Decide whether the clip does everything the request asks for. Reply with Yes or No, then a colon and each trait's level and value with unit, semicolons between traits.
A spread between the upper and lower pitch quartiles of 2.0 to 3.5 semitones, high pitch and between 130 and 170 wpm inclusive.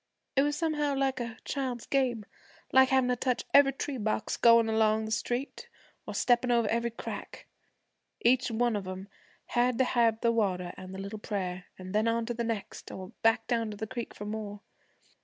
No: average, 2.8 semitones; high, 230 Hz; average, 195 wpm